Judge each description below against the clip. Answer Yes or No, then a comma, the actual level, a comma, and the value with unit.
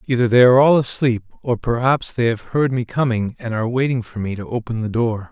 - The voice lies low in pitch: Yes, low, 120 Hz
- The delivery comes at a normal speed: No, fast, 235 wpm